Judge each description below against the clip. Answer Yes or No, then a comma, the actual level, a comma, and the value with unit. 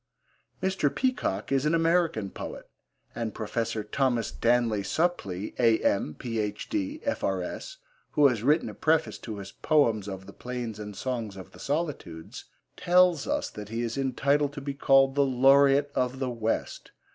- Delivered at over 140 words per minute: Yes, average, 155 wpm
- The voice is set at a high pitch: No, low, 130 Hz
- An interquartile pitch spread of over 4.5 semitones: Yes, average, 5.3 semitones